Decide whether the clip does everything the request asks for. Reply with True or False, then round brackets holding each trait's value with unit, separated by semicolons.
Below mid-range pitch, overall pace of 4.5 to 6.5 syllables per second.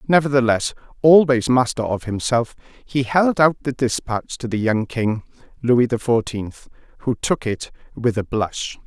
False (125 Hz; 4.3 syllables/s)